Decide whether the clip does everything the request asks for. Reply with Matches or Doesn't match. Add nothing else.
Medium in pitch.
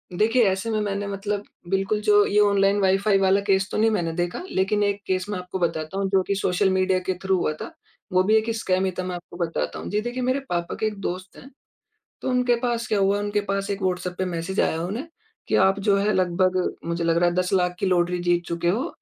Doesn't match